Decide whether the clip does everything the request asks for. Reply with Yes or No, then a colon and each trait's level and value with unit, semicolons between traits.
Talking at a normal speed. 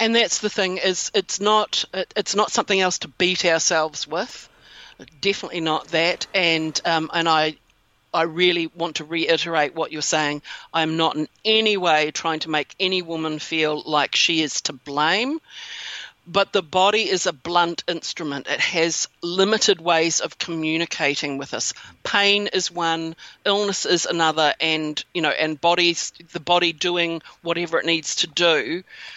Yes: average, 165 wpm